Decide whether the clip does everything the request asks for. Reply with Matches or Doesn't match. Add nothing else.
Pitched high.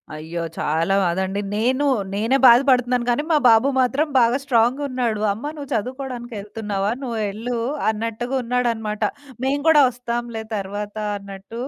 Matches